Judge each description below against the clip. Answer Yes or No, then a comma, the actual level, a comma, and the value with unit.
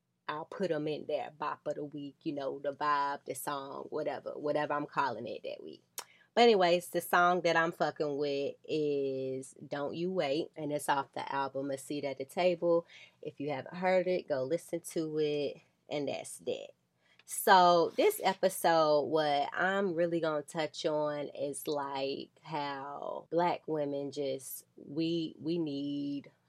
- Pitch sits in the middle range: Yes, medium, 150 Hz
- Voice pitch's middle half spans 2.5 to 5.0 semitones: Yes, average, 3.4 semitones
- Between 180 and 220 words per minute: No, average, 170 wpm